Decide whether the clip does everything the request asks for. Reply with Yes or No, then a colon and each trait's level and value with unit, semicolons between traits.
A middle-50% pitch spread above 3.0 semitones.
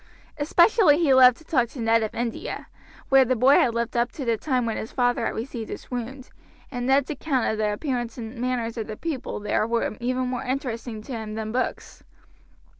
No: narrow, 2.5 semitones